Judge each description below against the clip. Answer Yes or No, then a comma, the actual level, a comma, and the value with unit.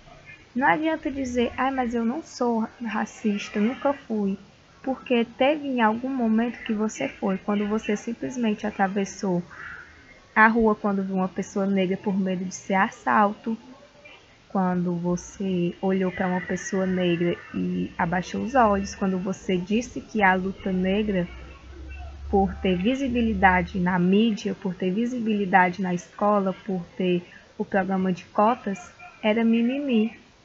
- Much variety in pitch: No, average, 3.6 semitones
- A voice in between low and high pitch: No, high, 200 Hz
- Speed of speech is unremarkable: Yes, average, 140 wpm